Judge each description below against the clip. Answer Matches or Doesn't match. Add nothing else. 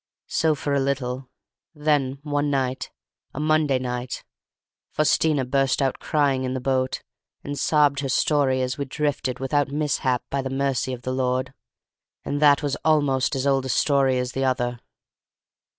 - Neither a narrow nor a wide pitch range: Doesn't match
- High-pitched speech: Doesn't match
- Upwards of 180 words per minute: Doesn't match